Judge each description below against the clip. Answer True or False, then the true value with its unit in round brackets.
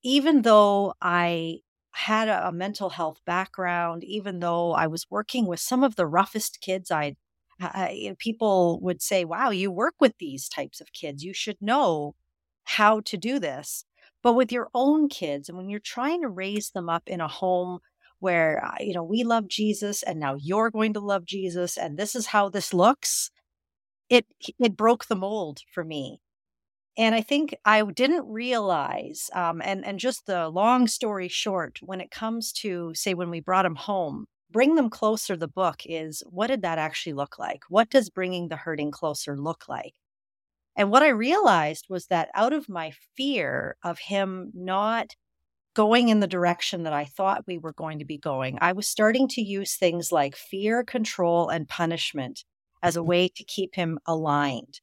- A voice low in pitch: False (190 Hz)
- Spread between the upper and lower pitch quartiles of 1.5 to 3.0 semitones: False (4.6 semitones)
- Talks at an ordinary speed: True (185 wpm)